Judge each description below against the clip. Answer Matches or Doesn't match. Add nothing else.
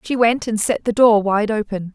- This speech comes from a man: Doesn't match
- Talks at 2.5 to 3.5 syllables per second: Doesn't match